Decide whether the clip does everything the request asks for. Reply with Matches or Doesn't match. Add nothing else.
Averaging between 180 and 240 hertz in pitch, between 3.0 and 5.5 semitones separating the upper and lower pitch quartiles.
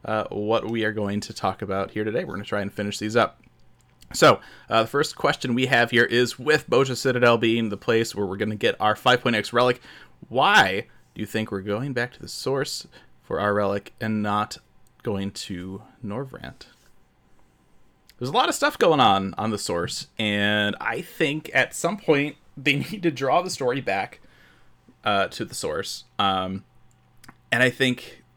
Doesn't match